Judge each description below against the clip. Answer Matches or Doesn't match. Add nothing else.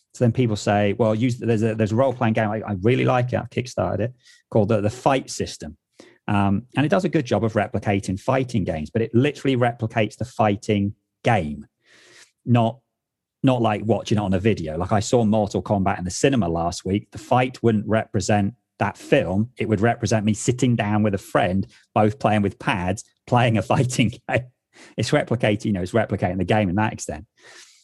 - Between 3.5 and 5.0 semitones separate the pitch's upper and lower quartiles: Doesn't match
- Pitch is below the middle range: Matches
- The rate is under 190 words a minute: Doesn't match